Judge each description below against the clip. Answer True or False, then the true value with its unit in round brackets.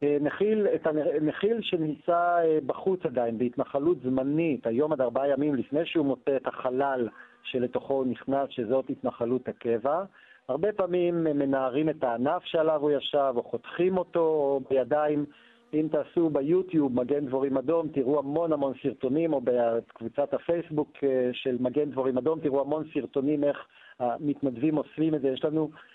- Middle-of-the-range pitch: True (145 Hz)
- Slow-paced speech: False (145 wpm)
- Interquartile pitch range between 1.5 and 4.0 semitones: True (3.1 semitones)